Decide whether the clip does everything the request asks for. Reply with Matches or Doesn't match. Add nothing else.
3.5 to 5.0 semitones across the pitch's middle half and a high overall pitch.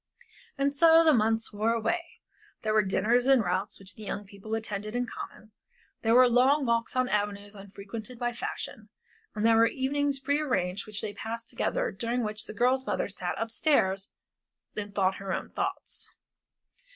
Matches